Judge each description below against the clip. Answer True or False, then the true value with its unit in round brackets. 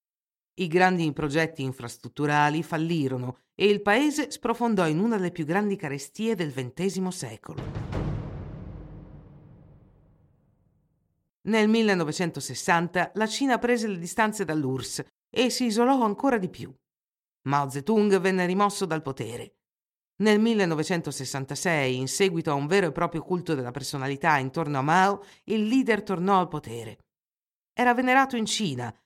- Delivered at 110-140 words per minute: True (130 wpm)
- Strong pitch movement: True (6.5 semitones)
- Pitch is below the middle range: False (175 Hz)